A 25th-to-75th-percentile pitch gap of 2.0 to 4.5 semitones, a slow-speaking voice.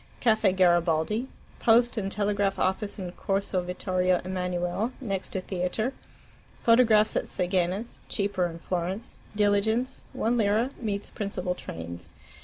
Yes: average, 3.2 semitones; slow, 125 wpm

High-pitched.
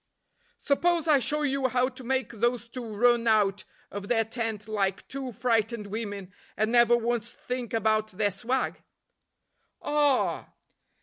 Yes: high, 235 Hz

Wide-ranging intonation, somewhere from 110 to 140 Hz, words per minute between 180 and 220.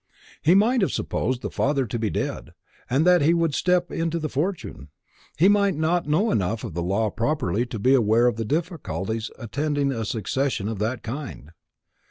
Yes: wide, 6.9 semitones; low, 135 Hz; average, 195 wpm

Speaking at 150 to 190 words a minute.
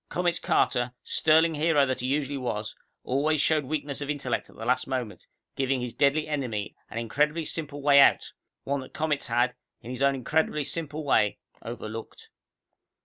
Yes: average, 170 wpm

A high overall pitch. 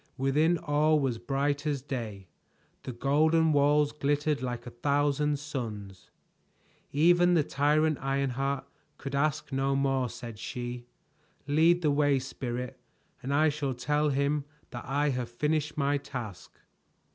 No: medium, 140 Hz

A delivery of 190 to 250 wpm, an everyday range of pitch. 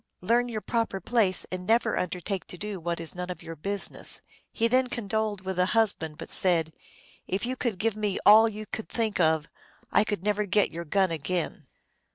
Yes: fast, 205 wpm; average, 3.5 semitones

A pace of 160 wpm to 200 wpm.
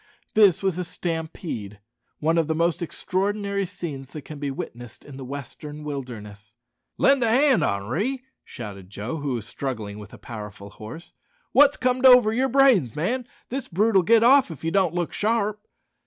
Yes: average, 170 wpm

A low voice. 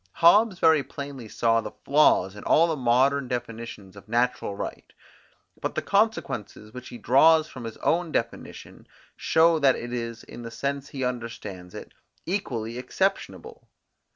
Yes: low, 125 Hz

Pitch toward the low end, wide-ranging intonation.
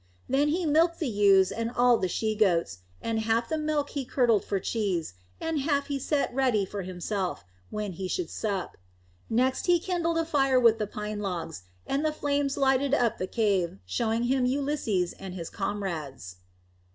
No: high, 230 Hz; wide, 6.5 semitones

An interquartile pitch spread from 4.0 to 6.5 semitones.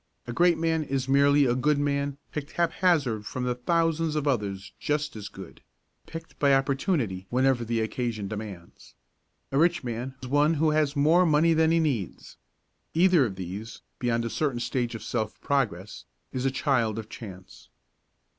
Yes: average, 4.9 semitones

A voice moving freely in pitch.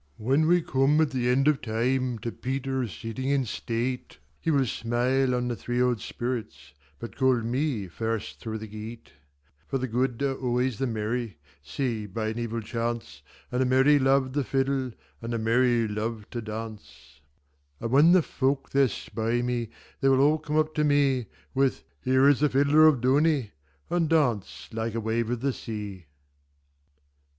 No: average, 3.4 semitones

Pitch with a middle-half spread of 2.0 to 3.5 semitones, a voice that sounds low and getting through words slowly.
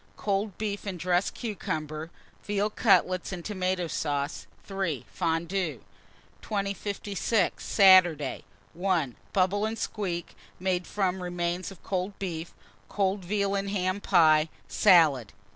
No: average, 2.8 semitones; medium, 185 Hz; slow, 115 wpm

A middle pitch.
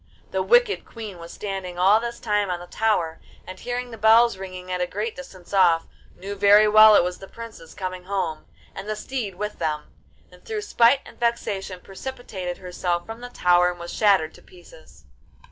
No: high, 195 Hz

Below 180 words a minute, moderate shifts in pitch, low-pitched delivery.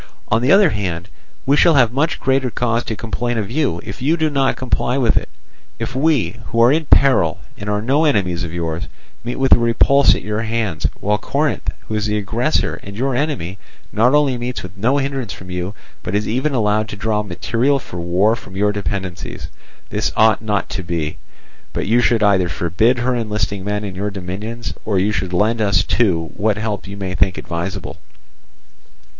No: average, 200 wpm; average, 4.5 semitones; low, 110 Hz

